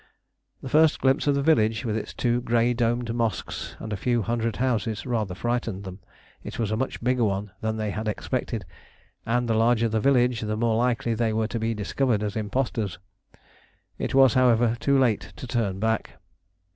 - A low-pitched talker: Yes, low, 115 Hz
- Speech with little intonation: Yes, narrow, 2.1 semitones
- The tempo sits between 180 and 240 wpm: Yes, average, 190 wpm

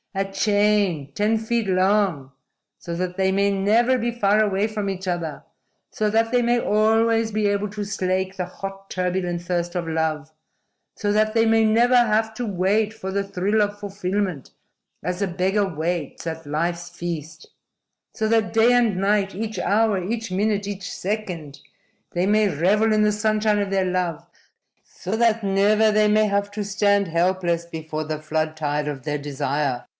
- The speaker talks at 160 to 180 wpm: Yes, average, 175 wpm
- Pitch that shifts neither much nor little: Yes, average, 3.6 semitones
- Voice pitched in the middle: No, high, 195 Hz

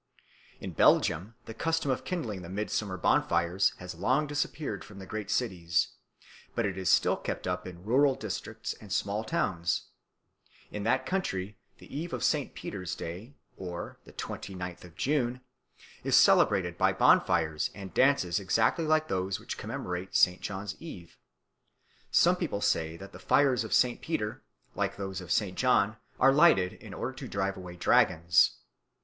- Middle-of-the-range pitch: No, low, 100 Hz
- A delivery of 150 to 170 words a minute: Yes, average, 160 wpm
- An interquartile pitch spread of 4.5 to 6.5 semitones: Yes, wide, 5.6 semitones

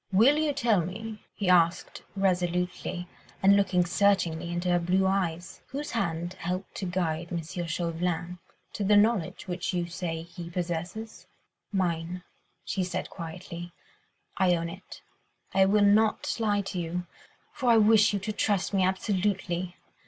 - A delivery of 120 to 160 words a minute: Yes, average, 145 wpm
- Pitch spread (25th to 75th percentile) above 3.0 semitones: No, average, 2.7 semitones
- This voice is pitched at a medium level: Yes, medium, 180 Hz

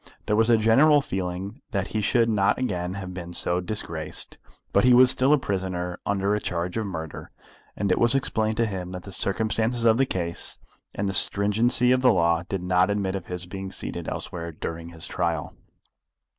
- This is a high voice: No, low, 100 Hz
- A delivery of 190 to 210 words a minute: Yes, average, 200 wpm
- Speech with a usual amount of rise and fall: Yes, average, 4.0 semitones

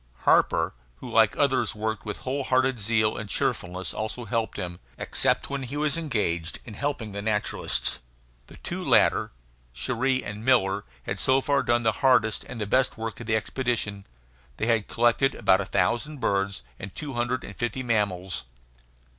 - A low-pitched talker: Yes, low, 110 Hz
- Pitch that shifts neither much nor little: Yes, average, 4.2 semitones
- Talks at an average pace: Yes, average, 175 wpm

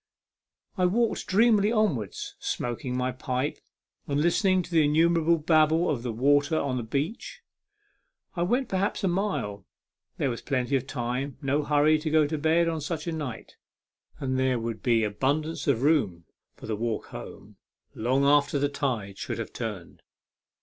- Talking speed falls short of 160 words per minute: No, average, 165 wpm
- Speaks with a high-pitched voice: No, medium, 145 Hz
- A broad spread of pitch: No, average, 4.7 semitones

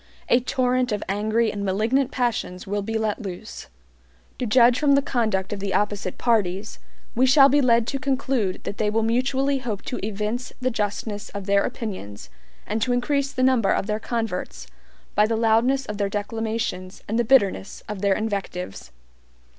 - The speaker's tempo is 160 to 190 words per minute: Yes, average, 180 wpm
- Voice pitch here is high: Yes, high, 220 Hz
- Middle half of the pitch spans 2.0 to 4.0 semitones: Yes, average, 3.6 semitones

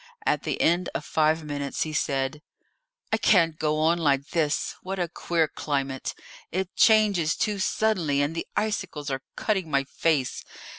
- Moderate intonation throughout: Yes, average, 4.1 semitones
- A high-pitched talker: No, medium, 160 Hz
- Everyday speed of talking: Yes, average, 160 wpm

